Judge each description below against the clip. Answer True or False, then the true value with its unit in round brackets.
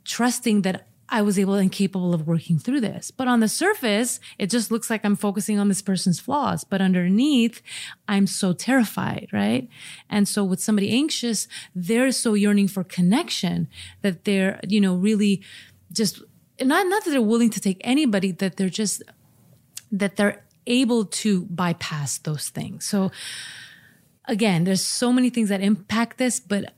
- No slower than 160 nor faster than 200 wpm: True (170 wpm)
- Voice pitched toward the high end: True (205 Hz)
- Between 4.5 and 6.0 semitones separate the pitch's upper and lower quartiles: False (3.6 semitones)